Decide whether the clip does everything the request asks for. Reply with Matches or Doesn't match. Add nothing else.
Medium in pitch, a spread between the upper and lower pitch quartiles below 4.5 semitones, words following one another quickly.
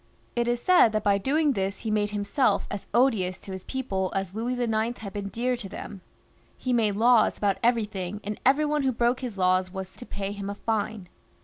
Doesn't match